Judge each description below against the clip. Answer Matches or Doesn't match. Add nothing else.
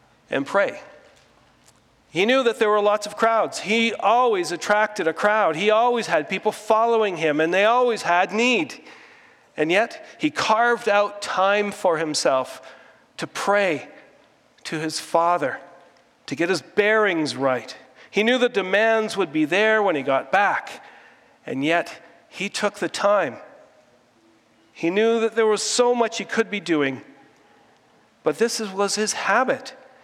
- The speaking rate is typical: Matches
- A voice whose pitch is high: Matches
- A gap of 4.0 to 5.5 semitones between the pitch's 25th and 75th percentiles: Matches